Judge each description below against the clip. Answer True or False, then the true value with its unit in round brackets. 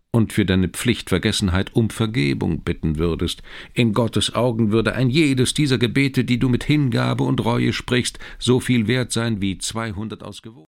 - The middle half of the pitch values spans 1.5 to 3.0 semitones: False (4.1 semitones)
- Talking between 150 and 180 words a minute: True (170 wpm)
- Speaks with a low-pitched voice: True (115 Hz)